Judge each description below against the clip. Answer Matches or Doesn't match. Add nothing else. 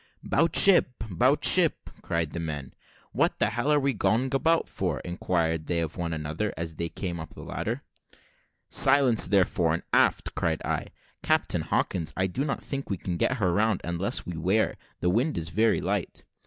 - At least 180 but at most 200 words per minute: Matches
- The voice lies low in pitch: Matches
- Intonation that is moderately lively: Doesn't match